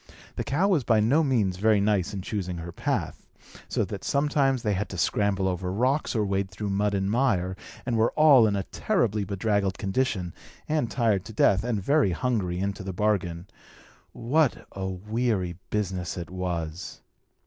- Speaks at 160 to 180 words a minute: Yes, average, 175 wpm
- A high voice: No, low, 100 Hz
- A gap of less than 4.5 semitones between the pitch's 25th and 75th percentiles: Yes, average, 4.1 semitones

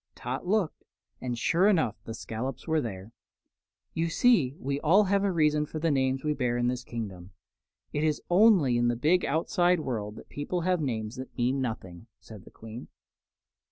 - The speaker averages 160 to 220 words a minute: Yes, average, 185 wpm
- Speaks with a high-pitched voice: No, low, 135 Hz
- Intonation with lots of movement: Yes, wide, 5.7 semitones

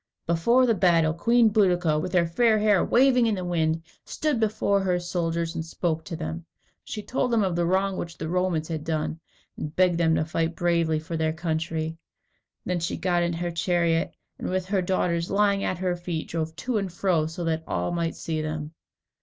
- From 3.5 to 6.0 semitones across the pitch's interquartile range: No, narrow, 2.6 semitones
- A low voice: No, medium, 170 Hz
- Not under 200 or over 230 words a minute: Yes, fast, 205 wpm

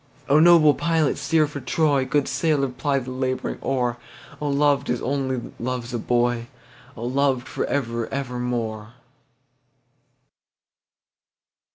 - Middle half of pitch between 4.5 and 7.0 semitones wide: No, average, 2.7 semitones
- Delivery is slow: Yes, slow, 105 wpm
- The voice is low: Yes, low, 130 Hz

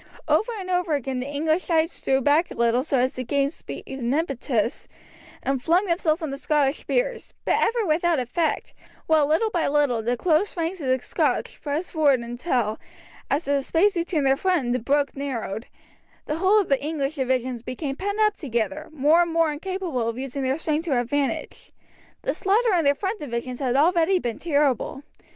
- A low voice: No, very high, 290 Hz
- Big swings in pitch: No, average, 4.6 semitones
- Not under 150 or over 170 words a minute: No, average, 195 wpm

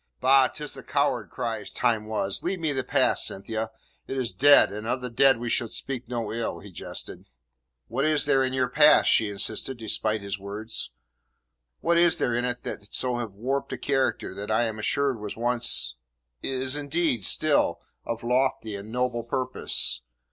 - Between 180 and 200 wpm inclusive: Yes, average, 185 wpm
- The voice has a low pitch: Yes, low, 120 Hz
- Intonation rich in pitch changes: No, average, 3.4 semitones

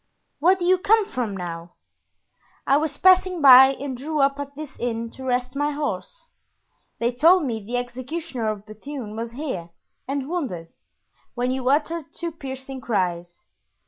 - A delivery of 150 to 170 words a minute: Yes, average, 160 wpm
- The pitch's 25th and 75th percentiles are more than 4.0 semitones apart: Yes, average, 4.6 semitones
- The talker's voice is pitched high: Yes, very high, 265 Hz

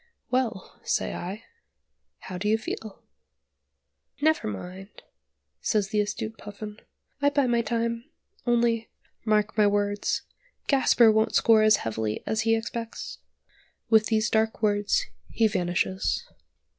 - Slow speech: Yes, slow, 125 wpm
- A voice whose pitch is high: Yes, high, 215 Hz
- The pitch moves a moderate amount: No, narrow, 2.1 semitones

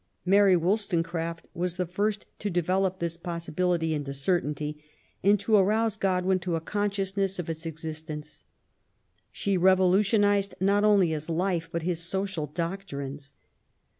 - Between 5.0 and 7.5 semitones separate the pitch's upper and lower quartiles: No, average, 3.2 semitones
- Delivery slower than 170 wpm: Yes, slow, 135 wpm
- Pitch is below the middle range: No, medium, 180 Hz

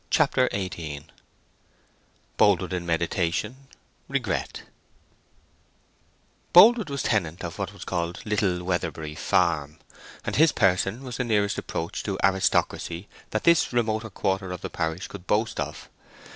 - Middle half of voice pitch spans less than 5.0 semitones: Yes, average, 4.5 semitones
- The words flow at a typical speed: No, slow, 125 wpm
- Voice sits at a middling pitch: No, very low, 95 Hz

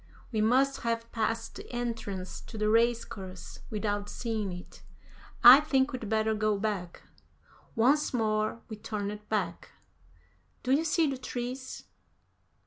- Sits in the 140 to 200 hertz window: No, high, 225 Hz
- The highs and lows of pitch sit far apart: No, average, 2.8 semitones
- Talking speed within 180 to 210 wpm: No, slow, 135 wpm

